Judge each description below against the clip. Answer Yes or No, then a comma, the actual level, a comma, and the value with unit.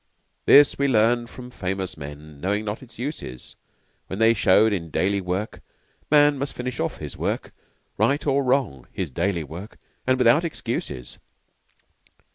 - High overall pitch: No, low, 110 Hz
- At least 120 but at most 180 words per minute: Yes, average, 150 wpm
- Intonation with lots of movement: Yes, wide, 6.2 semitones